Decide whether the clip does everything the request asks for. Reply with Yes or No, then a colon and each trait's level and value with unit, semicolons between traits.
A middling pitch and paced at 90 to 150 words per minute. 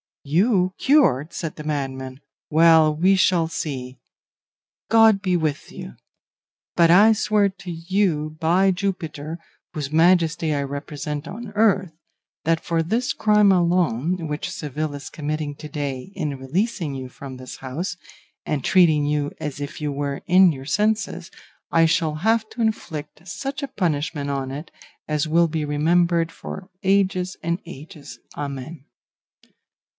Yes: medium, 160 Hz; average, 145 wpm